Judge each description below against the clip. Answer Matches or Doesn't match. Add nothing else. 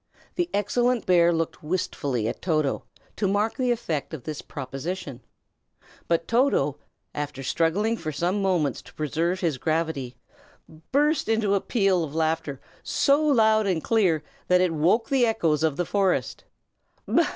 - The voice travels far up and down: Matches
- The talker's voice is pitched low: Doesn't match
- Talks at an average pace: Matches